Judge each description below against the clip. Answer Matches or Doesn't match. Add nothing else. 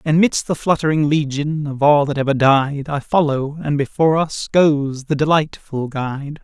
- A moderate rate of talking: Matches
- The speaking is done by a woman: Doesn't match